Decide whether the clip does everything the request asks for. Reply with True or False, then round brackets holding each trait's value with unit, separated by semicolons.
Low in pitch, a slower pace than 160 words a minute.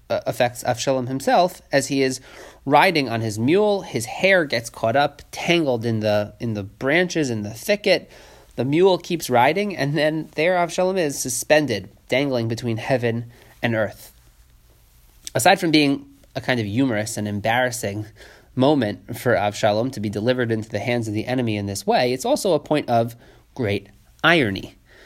False (125 Hz; 170 wpm)